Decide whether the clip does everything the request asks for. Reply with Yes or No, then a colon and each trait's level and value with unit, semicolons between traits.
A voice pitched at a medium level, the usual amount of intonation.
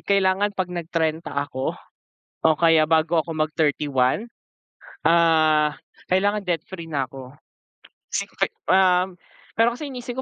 Yes: medium, 165 Hz; average, 3.5 semitones